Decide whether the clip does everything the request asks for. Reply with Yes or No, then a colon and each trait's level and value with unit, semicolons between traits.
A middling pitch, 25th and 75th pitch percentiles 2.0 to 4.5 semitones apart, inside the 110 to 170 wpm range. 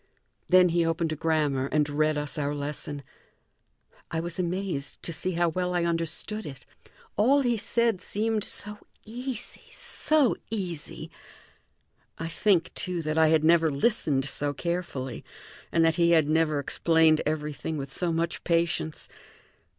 Yes: medium, 165 Hz; average, 3.1 semitones; average, 150 wpm